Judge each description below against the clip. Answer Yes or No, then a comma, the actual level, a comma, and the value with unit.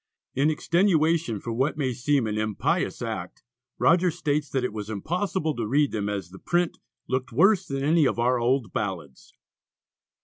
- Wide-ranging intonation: Yes, wide, 6.4 semitones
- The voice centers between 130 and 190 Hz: Yes, low, 135 Hz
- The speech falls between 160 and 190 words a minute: Yes, average, 170 wpm